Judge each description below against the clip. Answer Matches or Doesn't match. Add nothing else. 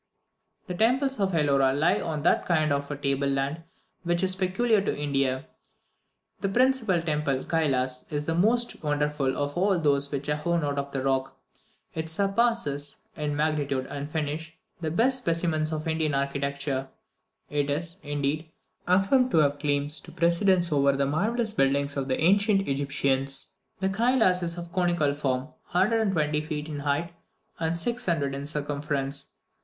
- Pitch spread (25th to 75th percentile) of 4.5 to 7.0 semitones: Doesn't match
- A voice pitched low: Doesn't match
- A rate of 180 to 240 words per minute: Doesn't match